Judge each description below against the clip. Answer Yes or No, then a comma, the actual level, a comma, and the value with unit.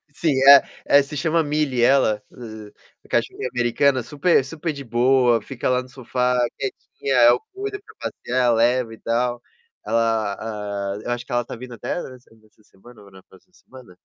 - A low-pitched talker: Yes, low, 125 Hz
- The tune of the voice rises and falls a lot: No, average, 2.9 semitones